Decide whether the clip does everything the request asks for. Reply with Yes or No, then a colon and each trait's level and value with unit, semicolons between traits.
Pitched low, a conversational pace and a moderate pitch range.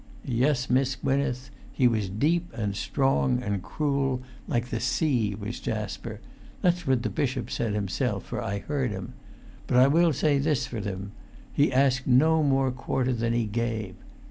Yes: low, 125 Hz; average, 170 wpm; average, 3.9 semitones